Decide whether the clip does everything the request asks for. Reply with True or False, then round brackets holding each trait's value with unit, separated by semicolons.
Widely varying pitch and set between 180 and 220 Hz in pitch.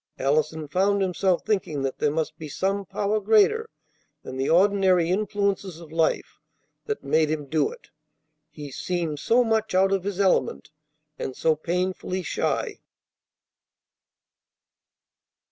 False (4.3 semitones; 185 Hz)